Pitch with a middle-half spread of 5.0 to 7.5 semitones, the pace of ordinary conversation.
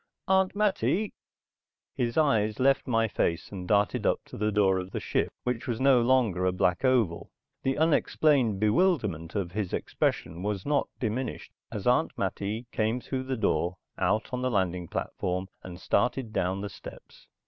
Yes: wide, 5.6 semitones; average, 170 wpm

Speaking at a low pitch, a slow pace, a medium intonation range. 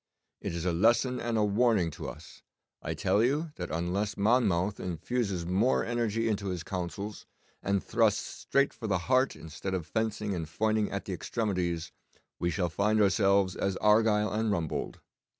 No: low, 100 Hz; average, 170 wpm; average, 3.9 semitones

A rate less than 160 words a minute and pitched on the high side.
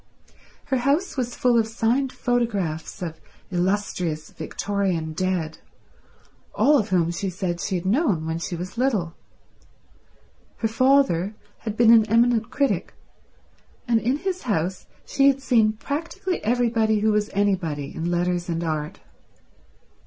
Yes: average, 140 wpm; high, 210 Hz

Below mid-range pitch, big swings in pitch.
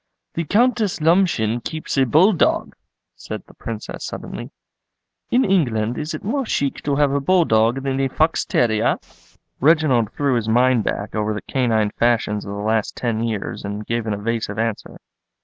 Yes: low, 120 Hz; wide, 6.0 semitones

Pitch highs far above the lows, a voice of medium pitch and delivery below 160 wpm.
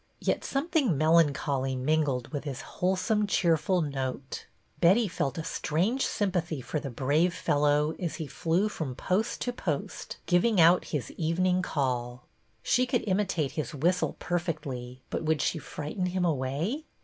No: average, 4.5 semitones; medium, 160 Hz; average, 150 wpm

